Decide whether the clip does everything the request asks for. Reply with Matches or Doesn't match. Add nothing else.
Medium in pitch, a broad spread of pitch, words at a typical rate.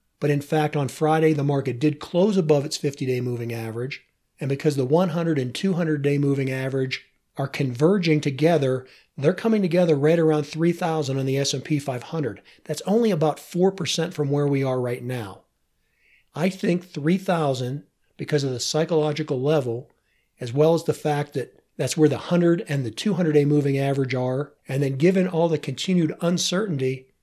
Doesn't match